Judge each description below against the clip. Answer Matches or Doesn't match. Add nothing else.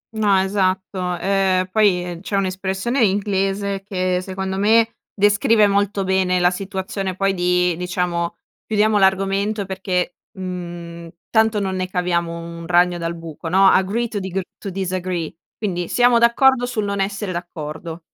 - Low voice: Doesn't match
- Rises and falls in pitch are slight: Matches